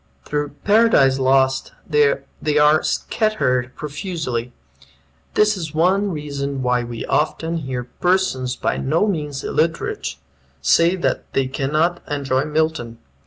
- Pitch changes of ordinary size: Yes, average, 4.1 semitones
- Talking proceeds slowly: Yes, slow, 120 wpm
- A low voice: No, medium, 150 Hz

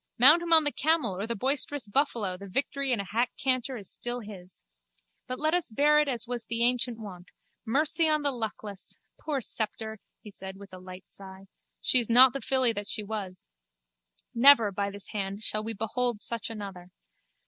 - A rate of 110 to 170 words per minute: No, average, 195 wpm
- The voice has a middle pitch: No, high, 230 Hz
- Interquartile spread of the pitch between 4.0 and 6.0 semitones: Yes, average, 4.8 semitones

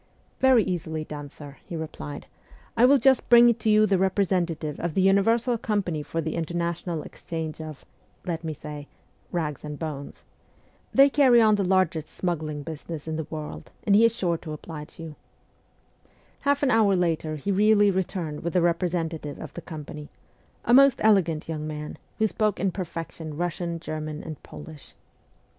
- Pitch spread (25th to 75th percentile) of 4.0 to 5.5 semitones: Yes, average, 4.5 semitones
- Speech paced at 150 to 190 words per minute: Yes, average, 175 wpm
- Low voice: No, medium, 170 Hz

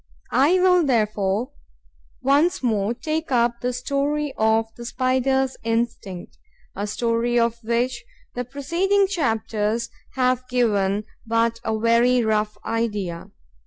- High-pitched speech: Yes, high, 235 Hz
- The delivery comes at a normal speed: No, slow, 120 wpm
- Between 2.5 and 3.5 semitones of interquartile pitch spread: Yes, average, 3.2 semitones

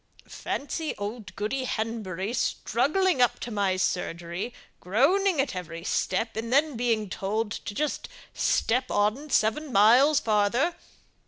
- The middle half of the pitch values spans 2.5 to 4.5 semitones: No, average, 5.0 semitones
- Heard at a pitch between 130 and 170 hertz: No, high, 225 Hz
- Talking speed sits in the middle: No, slow, 130 wpm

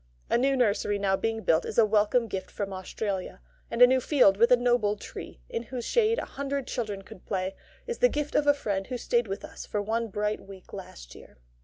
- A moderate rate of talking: No, fast, 225 wpm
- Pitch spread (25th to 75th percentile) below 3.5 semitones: No, average, 4.2 semitones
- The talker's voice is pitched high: Yes, high, 220 Hz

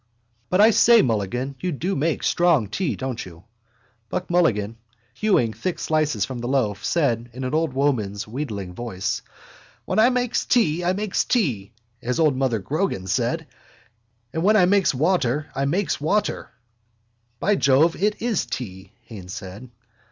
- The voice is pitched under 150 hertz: Yes, medium, 140 Hz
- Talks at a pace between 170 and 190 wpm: No, average, 160 wpm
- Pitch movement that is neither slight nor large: No, wide, 7.9 semitones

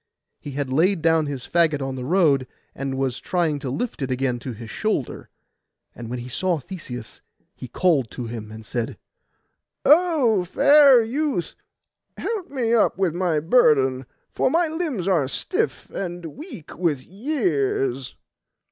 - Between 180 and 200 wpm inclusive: No, average, 155 wpm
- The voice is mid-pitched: Yes, medium, 160 Hz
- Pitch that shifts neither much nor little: No, wide, 8.7 semitones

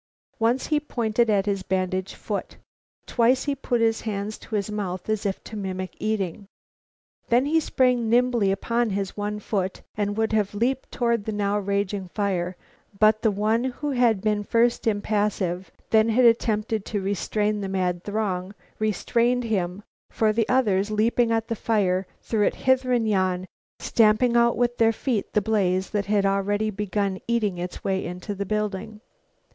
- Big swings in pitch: No, average, 2.8 semitones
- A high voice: Yes, high, 210 Hz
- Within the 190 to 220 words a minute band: No, average, 170 wpm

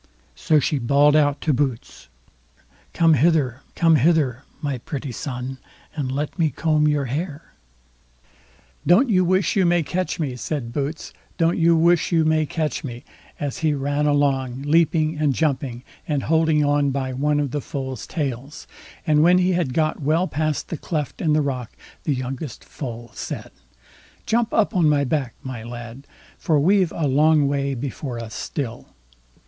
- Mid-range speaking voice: Yes, medium, 145 Hz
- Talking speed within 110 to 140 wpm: No, average, 165 wpm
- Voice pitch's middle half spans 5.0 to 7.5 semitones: No, average, 3.2 semitones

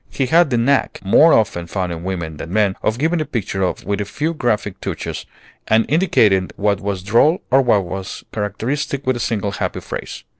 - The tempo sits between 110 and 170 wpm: No, average, 195 wpm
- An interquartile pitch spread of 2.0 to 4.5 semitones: No, wide, 5.6 semitones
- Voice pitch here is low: Yes, low, 105 Hz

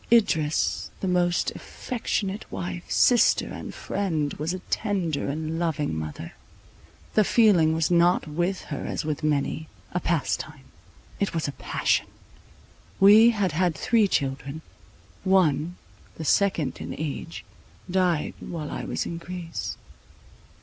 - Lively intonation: No, average, 4.0 semitones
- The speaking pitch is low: No, medium, 170 Hz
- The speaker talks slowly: Yes, slow, 130 wpm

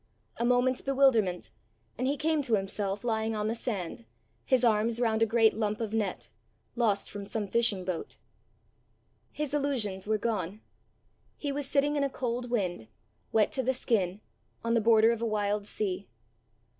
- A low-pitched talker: No, high, 225 Hz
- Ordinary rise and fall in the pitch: Yes, average, 3.3 semitones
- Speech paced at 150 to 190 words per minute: Yes, average, 170 wpm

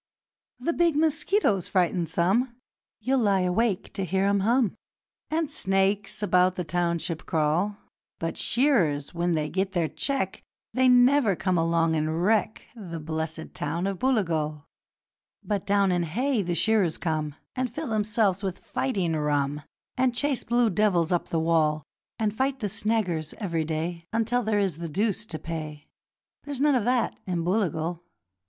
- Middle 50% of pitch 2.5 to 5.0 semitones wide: No, wide, 5.5 semitones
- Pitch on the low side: No, high, 190 Hz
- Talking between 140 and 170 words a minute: Yes, average, 160 wpm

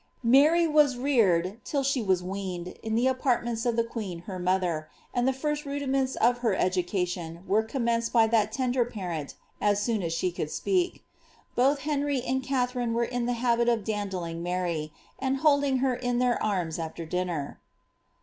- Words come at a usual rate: Yes, average, 175 wpm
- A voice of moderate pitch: No, high, 230 Hz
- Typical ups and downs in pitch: No, wide, 6.1 semitones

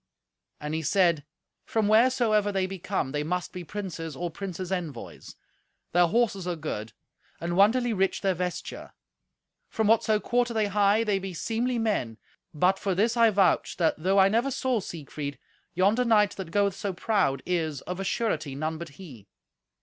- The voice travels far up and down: No, average, 4.5 semitones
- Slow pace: No, average, 175 wpm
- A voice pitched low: No, high, 190 Hz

